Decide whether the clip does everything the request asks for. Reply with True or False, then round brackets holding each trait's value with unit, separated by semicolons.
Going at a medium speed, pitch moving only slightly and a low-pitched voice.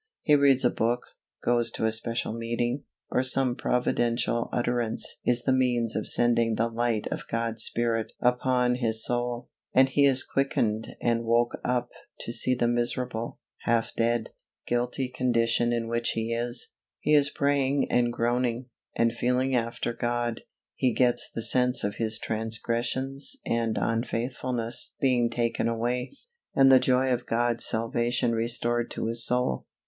True (155 wpm; 1.4 semitones; 120 Hz)